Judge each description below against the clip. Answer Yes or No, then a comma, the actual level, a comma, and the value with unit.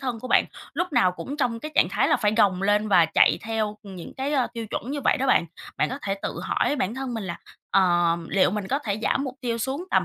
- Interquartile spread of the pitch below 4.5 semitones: No, average, 5.3 semitones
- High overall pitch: Yes, high, 225 Hz